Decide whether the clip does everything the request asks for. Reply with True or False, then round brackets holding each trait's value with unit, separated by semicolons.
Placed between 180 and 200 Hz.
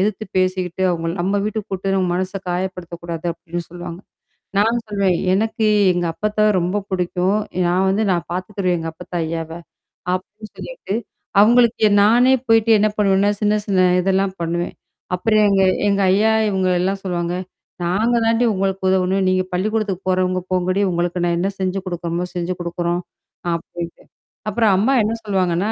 True (185 Hz)